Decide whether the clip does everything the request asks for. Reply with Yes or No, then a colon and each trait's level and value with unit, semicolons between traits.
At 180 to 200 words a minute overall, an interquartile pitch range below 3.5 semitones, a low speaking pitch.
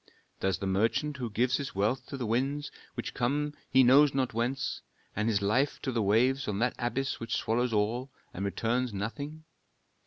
No: average, 185 wpm; average, 3.8 semitones; low, 120 Hz